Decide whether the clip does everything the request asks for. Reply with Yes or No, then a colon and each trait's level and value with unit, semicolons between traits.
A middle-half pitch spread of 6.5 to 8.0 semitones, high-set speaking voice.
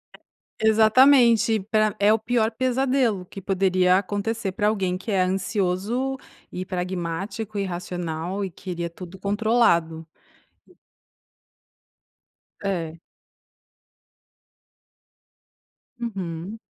No: average, 3.5 semitones; high, 195 Hz